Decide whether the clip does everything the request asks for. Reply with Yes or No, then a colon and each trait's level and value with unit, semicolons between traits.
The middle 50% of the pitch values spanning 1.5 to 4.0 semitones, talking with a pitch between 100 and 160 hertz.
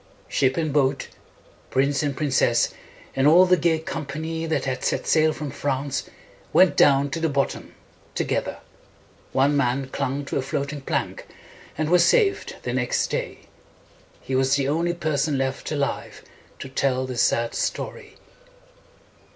Yes: average, 2.9 semitones; medium, 140 Hz